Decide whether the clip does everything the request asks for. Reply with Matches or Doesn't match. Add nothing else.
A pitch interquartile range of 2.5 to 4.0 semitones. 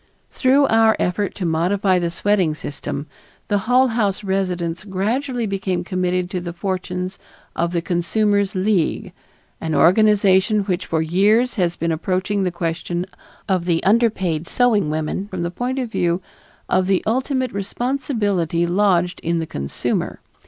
Matches